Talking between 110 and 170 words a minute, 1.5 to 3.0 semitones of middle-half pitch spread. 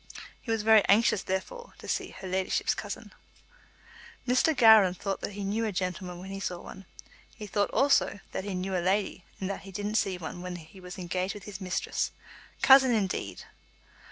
No: average, 190 wpm; narrow, 2.5 semitones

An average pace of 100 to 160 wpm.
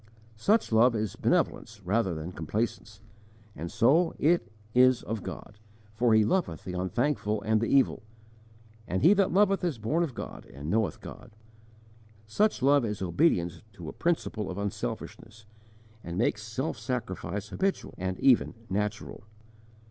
Yes: average, 150 wpm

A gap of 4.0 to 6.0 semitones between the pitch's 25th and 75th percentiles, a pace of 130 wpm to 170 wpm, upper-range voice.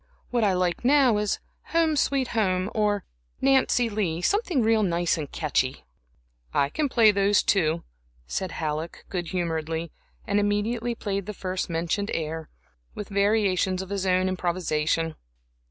Yes: average, 4.3 semitones; average, 145 wpm; high, 195 Hz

